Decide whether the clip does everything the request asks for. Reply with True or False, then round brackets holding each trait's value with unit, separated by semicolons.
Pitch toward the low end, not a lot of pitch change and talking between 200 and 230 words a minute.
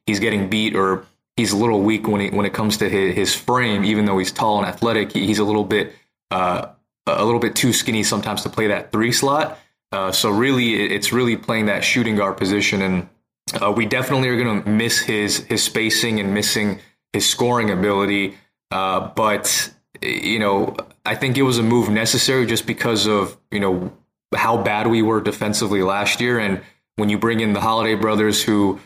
True (105 Hz; 2.2 semitones; 205 wpm)